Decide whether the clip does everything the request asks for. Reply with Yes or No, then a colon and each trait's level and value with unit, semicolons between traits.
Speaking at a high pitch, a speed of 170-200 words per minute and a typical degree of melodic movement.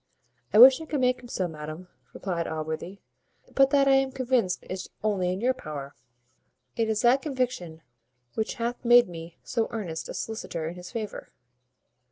No: high, 215 Hz; average, 175 wpm; wide, 6.6 semitones